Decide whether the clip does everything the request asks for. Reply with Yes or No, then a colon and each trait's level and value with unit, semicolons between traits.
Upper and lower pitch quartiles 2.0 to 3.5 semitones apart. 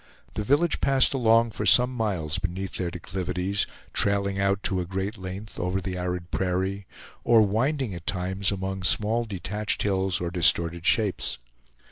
Yes: average, 2.8 semitones